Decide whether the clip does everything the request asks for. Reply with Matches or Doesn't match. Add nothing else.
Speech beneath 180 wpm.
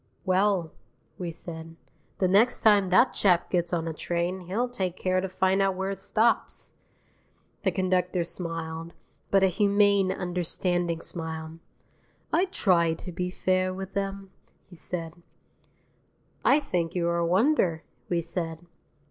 Matches